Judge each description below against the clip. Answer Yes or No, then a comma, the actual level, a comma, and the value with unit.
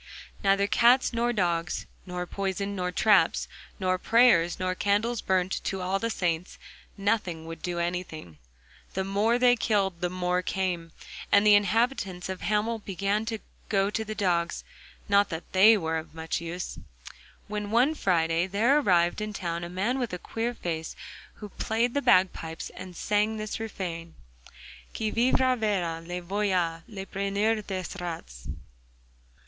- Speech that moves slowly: No, average, 155 wpm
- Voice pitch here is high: Yes, high, 195 Hz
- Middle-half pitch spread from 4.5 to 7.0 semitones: No, average, 3.4 semitones